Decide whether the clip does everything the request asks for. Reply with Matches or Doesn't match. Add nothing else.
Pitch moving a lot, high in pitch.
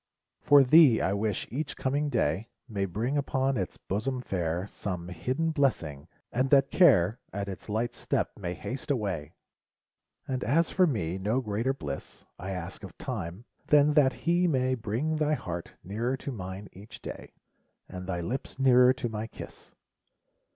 Doesn't match